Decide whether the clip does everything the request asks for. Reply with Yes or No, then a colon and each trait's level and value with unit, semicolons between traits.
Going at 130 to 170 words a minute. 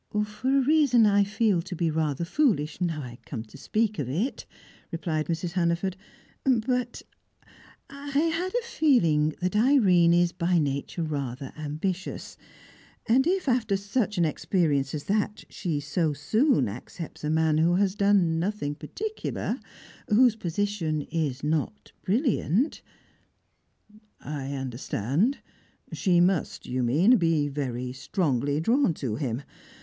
Yes: slow, 135 wpm